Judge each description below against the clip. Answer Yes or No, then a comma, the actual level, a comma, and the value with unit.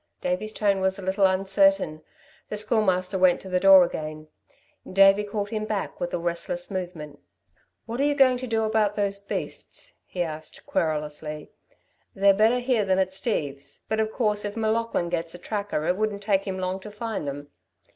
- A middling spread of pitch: Yes, average, 3.4 semitones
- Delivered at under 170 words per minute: No, average, 185 wpm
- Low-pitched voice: No, high, 195 Hz